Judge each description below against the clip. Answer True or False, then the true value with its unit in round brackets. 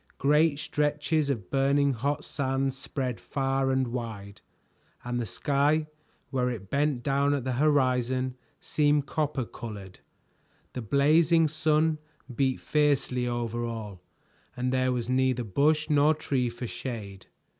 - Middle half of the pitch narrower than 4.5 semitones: True (3.3 semitones)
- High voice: False (135 Hz)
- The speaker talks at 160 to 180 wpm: False (135 wpm)